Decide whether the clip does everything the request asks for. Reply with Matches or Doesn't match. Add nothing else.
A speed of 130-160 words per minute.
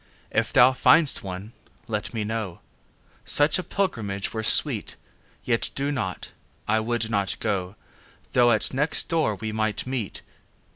Matches